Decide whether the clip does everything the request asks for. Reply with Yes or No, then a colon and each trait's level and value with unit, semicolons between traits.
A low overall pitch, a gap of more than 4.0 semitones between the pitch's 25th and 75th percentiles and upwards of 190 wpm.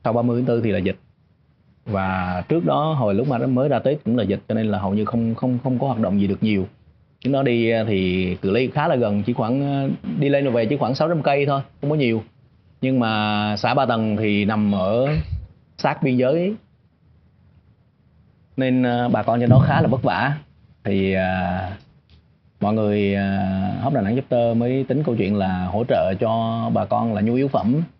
Yes: low, 115 Hz; average, 4.5 semitones; average, 215 wpm